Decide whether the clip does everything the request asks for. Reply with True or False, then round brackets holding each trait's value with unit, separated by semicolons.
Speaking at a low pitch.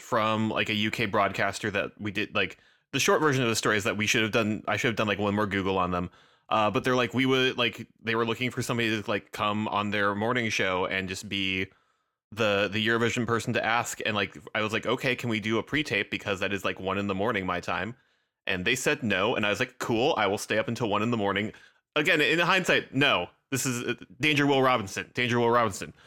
True (110 Hz)